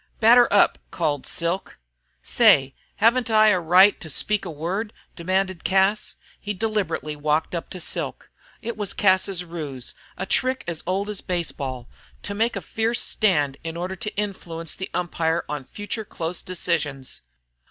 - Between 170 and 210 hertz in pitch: Yes, medium, 185 Hz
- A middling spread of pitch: Yes, average, 4.3 semitones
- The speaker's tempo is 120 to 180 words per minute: Yes, average, 155 wpm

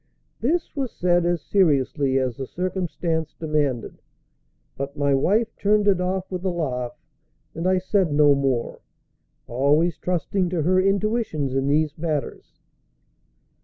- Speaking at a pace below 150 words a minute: Yes, slow, 135 wpm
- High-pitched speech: No, medium, 165 Hz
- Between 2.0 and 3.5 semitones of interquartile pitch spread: No, average, 4.8 semitones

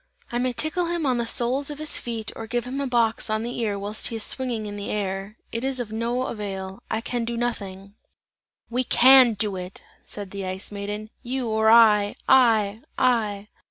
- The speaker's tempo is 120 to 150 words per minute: No, fast, 205 wpm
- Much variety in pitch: No, average, 3.1 semitones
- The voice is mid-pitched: No, high, 225 Hz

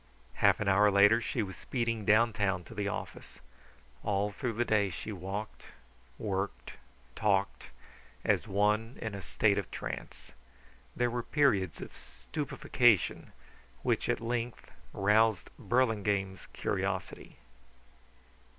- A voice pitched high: No, low, 105 Hz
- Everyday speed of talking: No, slow, 120 wpm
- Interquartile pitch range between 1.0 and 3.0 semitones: Yes, average, 2.7 semitones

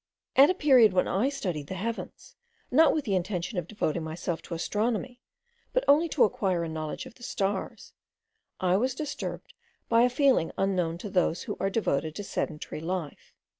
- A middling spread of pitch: No, wide, 6.4 semitones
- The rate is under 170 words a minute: No, average, 180 wpm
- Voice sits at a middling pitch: No, high, 195 Hz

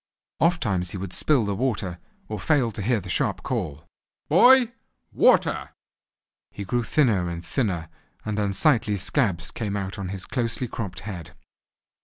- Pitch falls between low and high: No, low, 105 Hz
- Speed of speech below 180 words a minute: Yes, average, 150 wpm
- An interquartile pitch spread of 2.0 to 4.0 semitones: No, average, 5.0 semitones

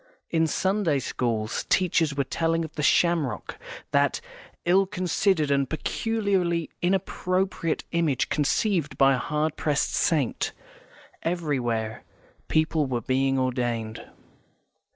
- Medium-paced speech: No, slow, 110 wpm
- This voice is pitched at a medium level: Yes, medium, 155 Hz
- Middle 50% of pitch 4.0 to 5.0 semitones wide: Yes, average, 4.6 semitones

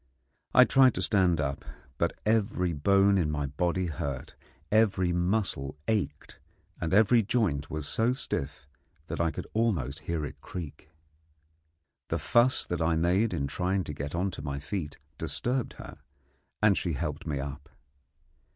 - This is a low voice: Yes, very low, 85 Hz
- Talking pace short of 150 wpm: No, average, 155 wpm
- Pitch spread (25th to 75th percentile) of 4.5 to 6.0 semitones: Yes, wide, 5.4 semitones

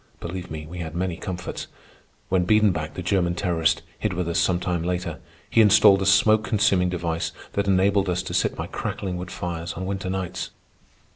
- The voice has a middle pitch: No, very low, 90 Hz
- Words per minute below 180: No, average, 195 wpm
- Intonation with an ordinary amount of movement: No, narrow, 2.1 semitones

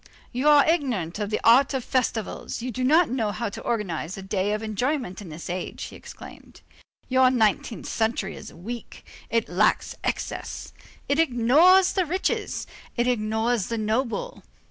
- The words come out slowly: No, average, 165 wpm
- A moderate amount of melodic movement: Yes, average, 3.9 semitones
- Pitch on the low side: No, high, 235 Hz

